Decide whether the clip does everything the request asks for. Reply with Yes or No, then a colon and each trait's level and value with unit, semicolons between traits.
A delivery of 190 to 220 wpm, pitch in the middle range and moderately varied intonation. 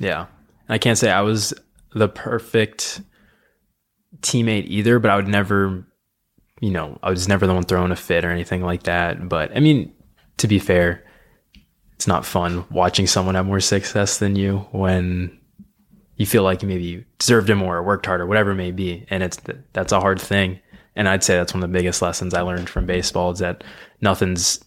No: average, 200 wpm; very low, 95 Hz; average, 3.0 semitones